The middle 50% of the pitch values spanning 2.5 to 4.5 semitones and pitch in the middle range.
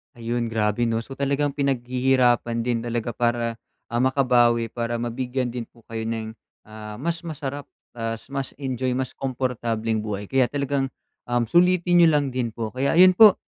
No: average, 2.8 semitones; low, 120 Hz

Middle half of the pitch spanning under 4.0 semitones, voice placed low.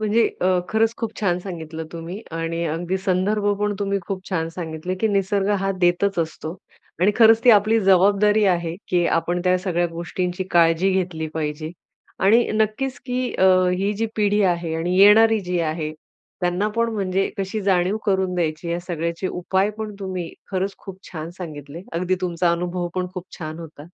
No: average, 3.0 semitones; medium, 185 Hz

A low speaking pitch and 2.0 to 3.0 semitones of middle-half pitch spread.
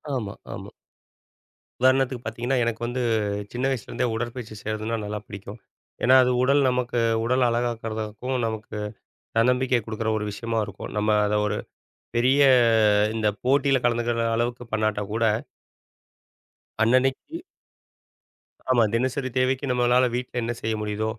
Yes: low, 120 Hz; narrow, 2.5 semitones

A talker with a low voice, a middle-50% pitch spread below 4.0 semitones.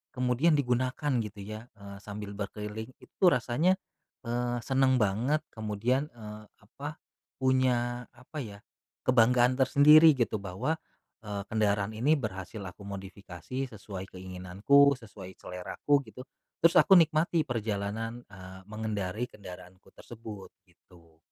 No: low, 110 Hz; average, 4.4 semitones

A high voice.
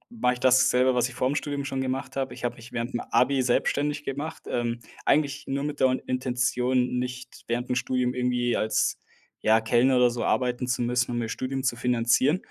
No: low, 125 Hz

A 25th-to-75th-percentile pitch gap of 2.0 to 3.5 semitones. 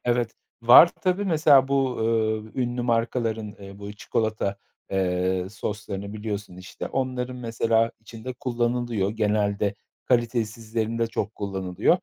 Yes: average, 2.9 semitones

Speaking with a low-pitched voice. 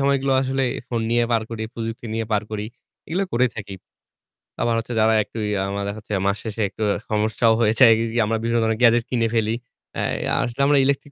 Yes: low, 115 Hz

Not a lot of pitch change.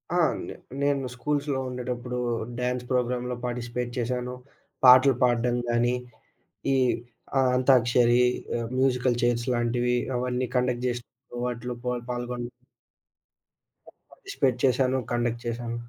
Yes: narrow, 0.9 semitones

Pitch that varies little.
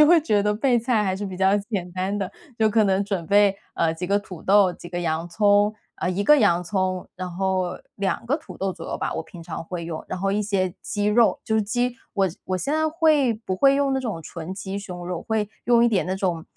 No: average, 3.2 semitones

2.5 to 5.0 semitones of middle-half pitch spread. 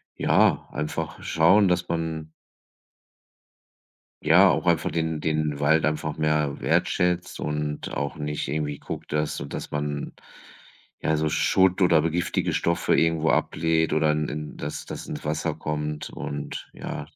No: narrow, 1.5 semitones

